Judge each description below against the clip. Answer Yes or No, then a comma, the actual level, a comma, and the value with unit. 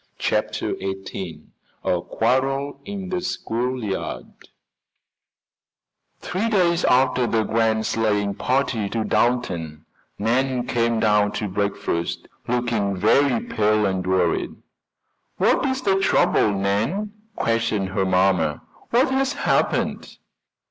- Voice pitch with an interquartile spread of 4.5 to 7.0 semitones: Yes, wide, 5.4 semitones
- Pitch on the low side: Yes, low, 115 Hz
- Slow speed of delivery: Yes, slow, 105 wpm